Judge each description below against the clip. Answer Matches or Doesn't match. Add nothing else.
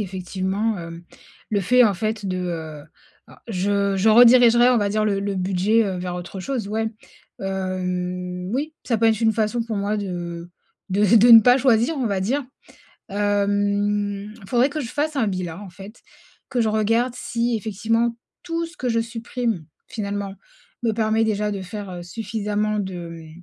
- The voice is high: Matches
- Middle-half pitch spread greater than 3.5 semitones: Doesn't match